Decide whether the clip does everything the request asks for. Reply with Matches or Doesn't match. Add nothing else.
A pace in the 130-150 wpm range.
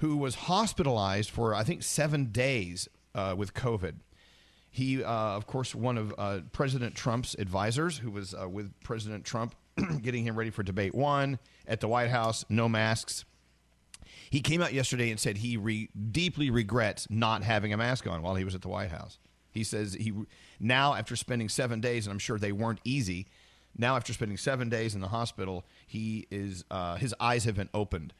Doesn't match